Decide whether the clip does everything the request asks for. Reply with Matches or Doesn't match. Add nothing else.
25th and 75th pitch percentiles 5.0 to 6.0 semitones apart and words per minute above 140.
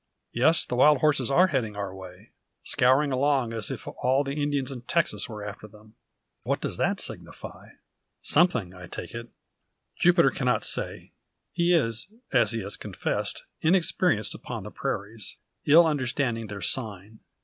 Matches